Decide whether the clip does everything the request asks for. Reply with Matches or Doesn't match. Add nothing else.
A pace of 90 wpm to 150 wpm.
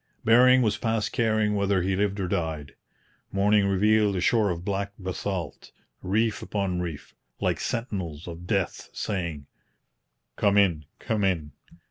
Matches